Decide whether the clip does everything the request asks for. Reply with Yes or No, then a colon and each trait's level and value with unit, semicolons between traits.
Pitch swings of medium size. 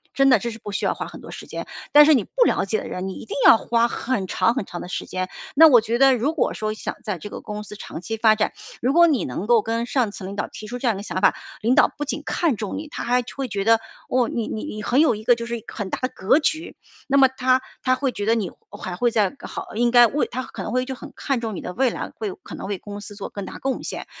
Yes: average, 4.0 semitones